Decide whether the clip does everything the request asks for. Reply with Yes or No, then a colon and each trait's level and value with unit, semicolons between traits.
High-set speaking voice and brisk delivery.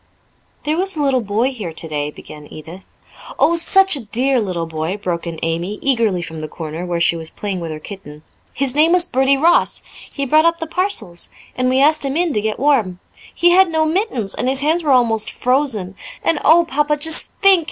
Yes: very high, 255 Hz; fast, 210 wpm